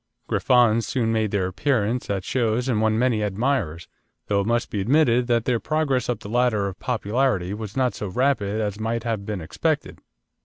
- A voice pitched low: Yes, low, 115 Hz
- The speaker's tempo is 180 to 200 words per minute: Yes, average, 190 wpm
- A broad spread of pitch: No, average, 3.4 semitones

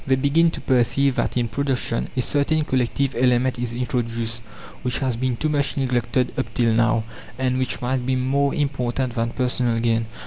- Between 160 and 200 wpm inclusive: Yes, average, 180 wpm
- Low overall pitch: Yes, low, 125 Hz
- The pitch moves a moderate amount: No, narrow, 2.2 semitones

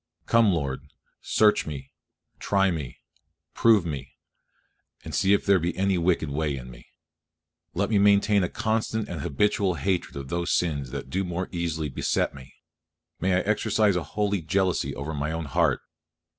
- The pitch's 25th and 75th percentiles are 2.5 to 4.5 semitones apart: No, average, 5.3 semitones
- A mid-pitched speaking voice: No, very low, 90 Hz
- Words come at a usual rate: Yes, average, 165 wpm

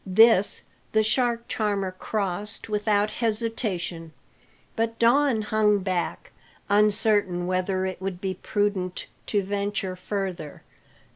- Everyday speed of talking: No, slow, 110 wpm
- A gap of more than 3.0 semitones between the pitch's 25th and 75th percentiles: No, average, 2.7 semitones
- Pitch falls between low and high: No, high, 205 Hz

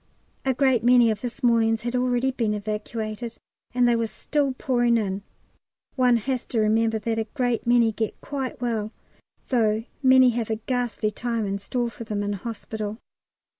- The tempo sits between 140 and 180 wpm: Yes, average, 170 wpm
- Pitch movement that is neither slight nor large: No, narrow, 2.2 semitones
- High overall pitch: Yes, high, 230 Hz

